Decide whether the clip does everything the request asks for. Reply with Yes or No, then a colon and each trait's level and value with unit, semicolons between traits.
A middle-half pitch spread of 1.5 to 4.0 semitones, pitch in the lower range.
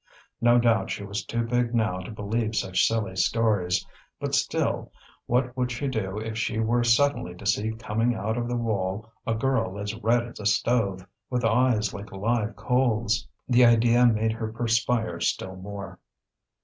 Yes: narrow, 2.5 semitones; low, 115 Hz